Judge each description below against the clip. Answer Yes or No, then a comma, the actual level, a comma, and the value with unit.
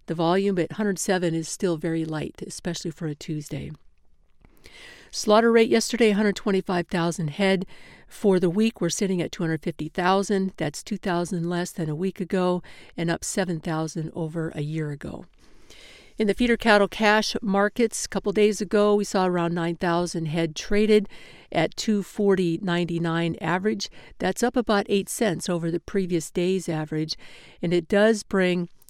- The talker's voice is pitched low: No, medium, 180 Hz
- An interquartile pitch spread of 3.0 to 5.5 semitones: Yes, average, 3.6 semitones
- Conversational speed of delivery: Yes, average, 145 wpm